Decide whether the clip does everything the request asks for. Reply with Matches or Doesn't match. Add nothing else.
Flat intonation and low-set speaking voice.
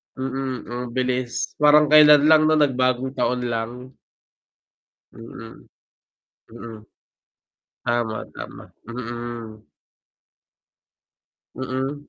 Matches